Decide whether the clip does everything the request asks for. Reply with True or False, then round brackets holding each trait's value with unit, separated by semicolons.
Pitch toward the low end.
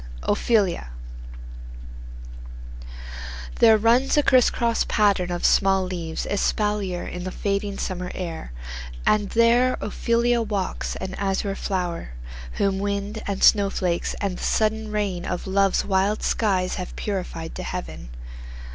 False (200 Hz)